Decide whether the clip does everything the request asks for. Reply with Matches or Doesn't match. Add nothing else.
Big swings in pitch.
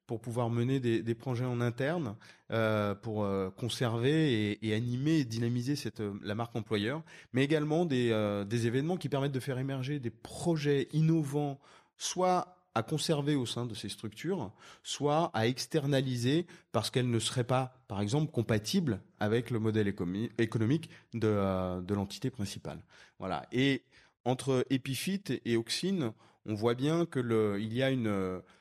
Doesn't match